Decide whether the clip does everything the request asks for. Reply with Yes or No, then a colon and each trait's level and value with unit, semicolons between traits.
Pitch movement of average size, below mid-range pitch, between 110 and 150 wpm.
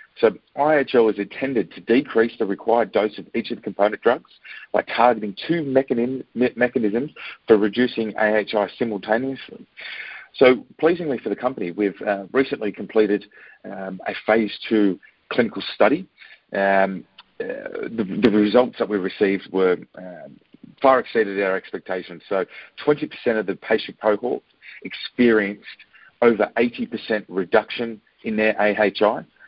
Yes: average, 3.3 semitones; low, 110 Hz; slow, 135 wpm